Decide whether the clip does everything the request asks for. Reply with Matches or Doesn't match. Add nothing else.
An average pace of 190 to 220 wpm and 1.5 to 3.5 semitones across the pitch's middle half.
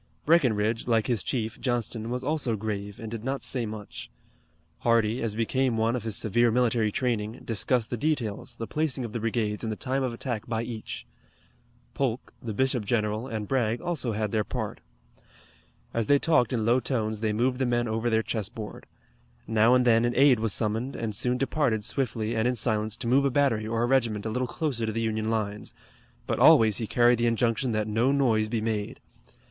Matches